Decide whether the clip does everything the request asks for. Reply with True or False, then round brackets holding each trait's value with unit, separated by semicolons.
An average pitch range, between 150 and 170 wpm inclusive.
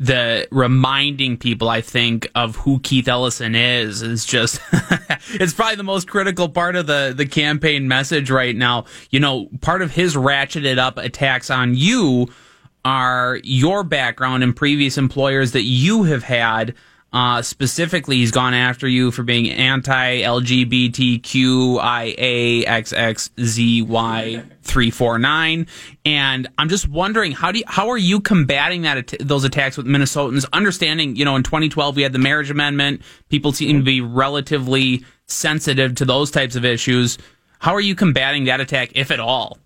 True (3.1 semitones; 155 wpm)